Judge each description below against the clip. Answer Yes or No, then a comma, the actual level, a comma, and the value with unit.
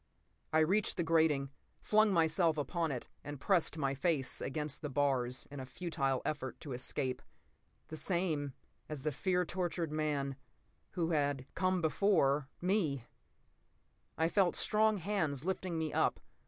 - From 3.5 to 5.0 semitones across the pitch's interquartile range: Yes, average, 4.2 semitones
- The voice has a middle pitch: Yes, medium, 155 Hz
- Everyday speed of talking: No, slow, 130 wpm